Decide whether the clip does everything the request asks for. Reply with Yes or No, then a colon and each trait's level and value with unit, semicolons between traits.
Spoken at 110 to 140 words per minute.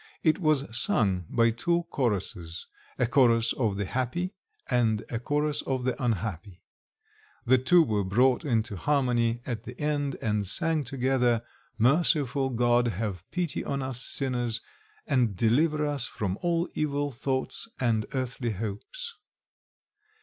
Yes: slow, 135 wpm